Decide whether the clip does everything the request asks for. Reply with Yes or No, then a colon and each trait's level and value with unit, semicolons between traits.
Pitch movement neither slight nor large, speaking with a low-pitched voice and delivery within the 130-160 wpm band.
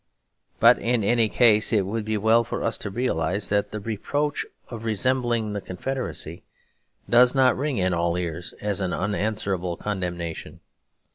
Yes: average, 4.0 semitones; low, 105 Hz; average, 155 wpm